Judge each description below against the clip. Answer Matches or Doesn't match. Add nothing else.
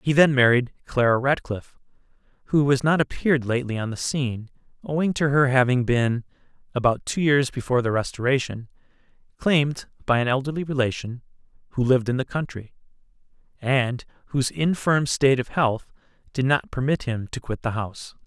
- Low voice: Matches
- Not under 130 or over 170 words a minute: Matches